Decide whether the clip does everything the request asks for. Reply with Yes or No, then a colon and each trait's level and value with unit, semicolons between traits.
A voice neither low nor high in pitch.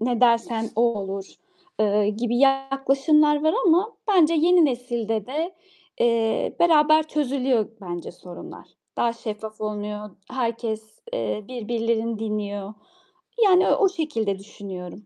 No: high, 235 Hz